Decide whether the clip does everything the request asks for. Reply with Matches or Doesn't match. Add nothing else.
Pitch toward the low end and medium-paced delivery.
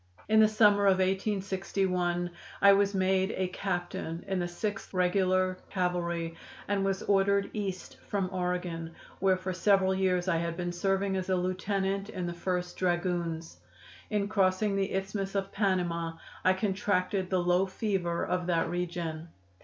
Doesn't match